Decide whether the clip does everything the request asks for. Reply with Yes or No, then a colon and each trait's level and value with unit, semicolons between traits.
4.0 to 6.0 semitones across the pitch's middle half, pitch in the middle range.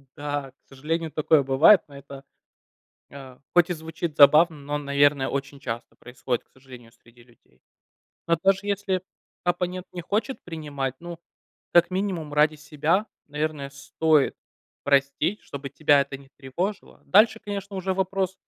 Yes: average, 4.3 semitones; medium, 150 Hz